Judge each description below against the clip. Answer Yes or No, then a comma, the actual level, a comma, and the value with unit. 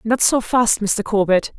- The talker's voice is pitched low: No, high, 215 Hz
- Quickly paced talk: No, average, 190 wpm